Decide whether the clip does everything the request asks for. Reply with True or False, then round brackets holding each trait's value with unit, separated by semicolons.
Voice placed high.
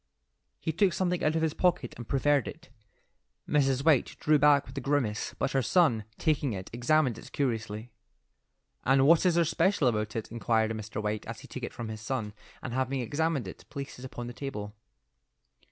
False (130 Hz)